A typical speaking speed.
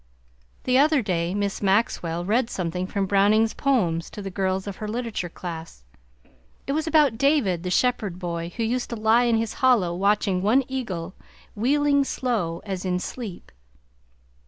Yes: average, 160 wpm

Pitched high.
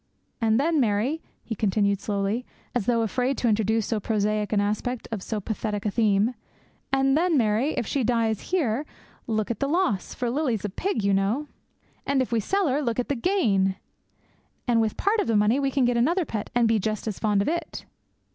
Yes: high, 230 Hz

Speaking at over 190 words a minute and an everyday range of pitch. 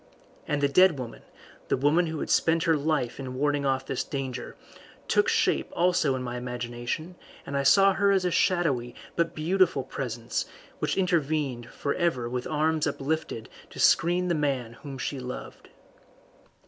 No: average, 165 wpm; average, 4.7 semitones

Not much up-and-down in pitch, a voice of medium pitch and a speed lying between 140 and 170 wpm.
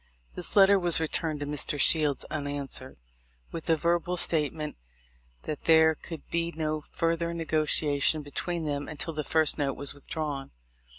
Yes: narrow, 2.3 semitones; medium, 155 Hz; average, 155 wpm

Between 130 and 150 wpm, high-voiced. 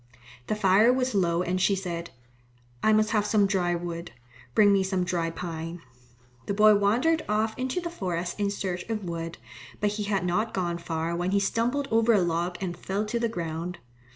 No: average, 195 wpm; high, 195 Hz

